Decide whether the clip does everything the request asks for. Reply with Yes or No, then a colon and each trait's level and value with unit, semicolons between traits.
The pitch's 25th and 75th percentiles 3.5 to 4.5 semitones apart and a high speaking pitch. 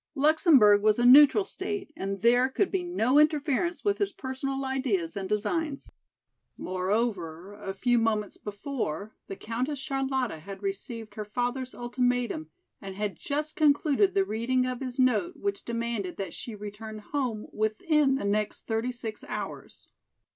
No: average, 5.0 semitones; high, 240 Hz